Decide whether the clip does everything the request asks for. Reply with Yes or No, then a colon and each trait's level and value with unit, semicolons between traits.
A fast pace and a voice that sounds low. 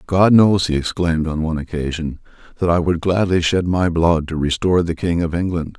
Yes: fast, 210 wpm; very low, 85 Hz